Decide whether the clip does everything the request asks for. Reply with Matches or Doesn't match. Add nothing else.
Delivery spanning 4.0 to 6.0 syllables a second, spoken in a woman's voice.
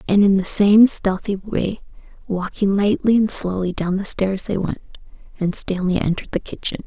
Matches